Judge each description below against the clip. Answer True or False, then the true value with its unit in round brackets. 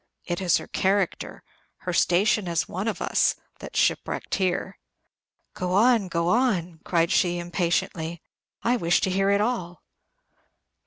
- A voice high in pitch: False (180 Hz)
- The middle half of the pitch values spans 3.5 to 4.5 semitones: False (2.6 semitones)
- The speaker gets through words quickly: False (145 wpm)